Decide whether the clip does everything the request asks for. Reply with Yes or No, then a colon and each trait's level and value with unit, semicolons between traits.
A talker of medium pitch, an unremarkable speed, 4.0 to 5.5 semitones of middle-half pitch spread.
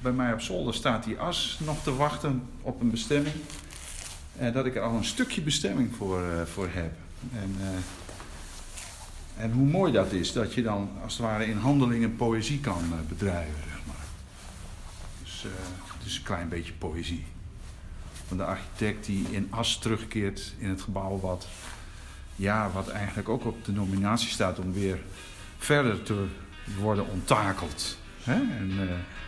No: very low, 95 Hz; average, 160 wpm; average, 4.5 semitones